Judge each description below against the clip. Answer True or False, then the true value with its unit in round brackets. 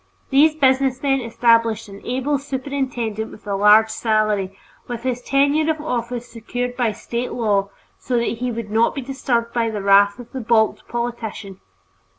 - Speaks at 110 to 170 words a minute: True (160 wpm)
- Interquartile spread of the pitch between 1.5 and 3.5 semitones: True (3.0 semitones)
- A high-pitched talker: True (235 Hz)